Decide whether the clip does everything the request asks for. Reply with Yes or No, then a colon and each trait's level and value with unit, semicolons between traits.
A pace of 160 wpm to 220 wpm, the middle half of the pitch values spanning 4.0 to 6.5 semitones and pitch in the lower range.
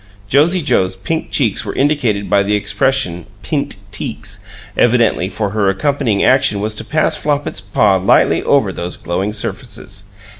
No: average, 150 wpm; wide, 5.6 semitones; low, 105 Hz